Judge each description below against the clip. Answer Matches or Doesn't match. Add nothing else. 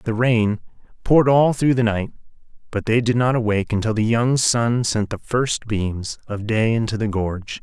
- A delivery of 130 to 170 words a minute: Doesn't match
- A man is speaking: Matches